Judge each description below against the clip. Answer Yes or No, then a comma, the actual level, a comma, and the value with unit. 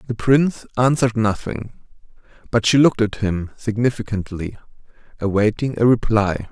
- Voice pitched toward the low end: Yes, low, 110 Hz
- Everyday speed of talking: No, slow, 120 wpm